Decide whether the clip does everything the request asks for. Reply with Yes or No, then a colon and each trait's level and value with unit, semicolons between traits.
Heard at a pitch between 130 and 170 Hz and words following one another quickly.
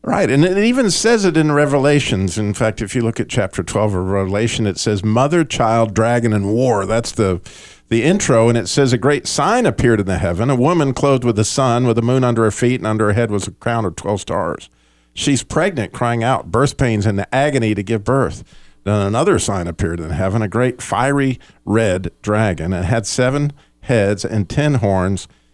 No: low, 115 Hz; fast, 215 wpm